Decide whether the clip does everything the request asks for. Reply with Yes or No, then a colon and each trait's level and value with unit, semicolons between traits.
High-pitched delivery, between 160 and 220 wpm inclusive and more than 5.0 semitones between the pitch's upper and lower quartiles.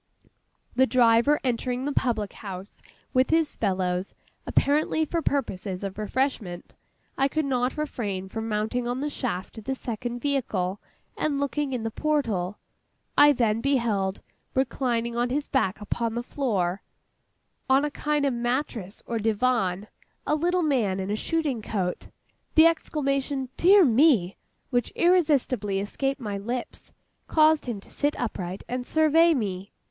No: high, 245 Hz; average, 150 wpm; wide, 5.4 semitones